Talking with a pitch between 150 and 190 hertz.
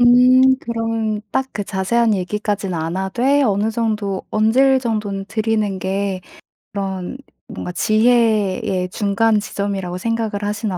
No: high, 210 Hz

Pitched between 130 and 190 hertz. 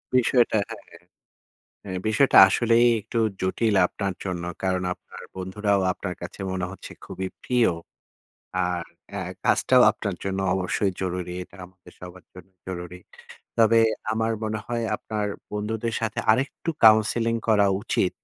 No: low, 100 Hz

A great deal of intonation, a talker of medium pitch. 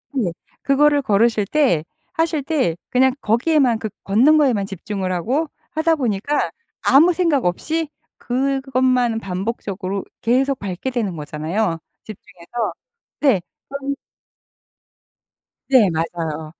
No: wide, 6.3 semitones; high, 235 Hz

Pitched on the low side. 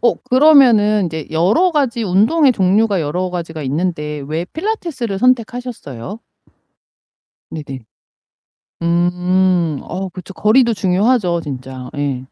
No: medium, 185 Hz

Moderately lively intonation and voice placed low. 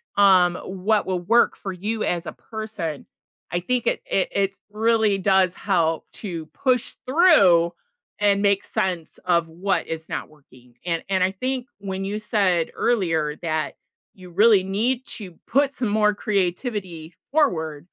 No: average, 4.0 semitones; high, 195 Hz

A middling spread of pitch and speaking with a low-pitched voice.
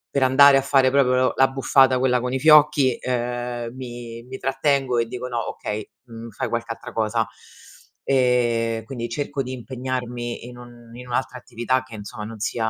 No: narrow, 1.9 semitones; low, 125 Hz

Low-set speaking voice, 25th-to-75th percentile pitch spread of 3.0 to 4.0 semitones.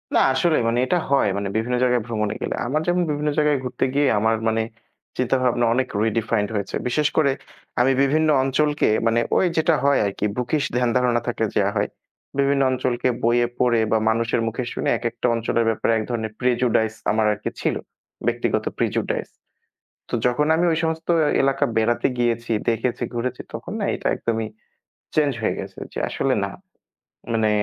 Yes: low, 120 Hz; average, 3.4 semitones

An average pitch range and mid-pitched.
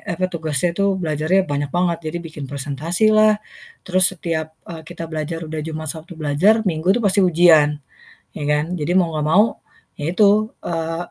Yes: average, 3.1 semitones; medium, 165 Hz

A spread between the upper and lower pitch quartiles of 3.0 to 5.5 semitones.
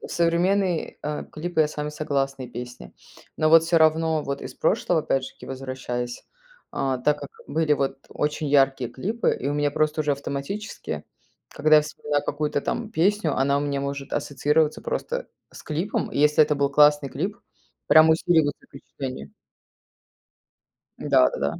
No: narrow, 2.6 semitones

